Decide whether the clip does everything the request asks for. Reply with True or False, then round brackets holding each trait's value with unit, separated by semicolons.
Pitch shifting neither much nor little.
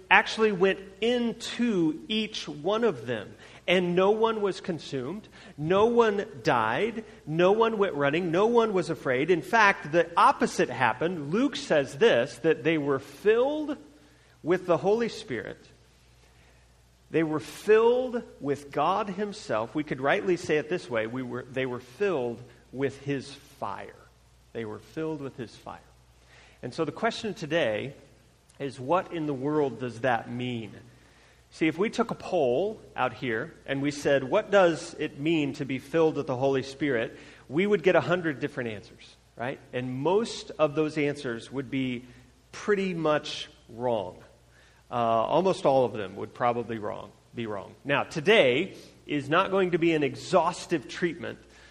False (7.1 semitones)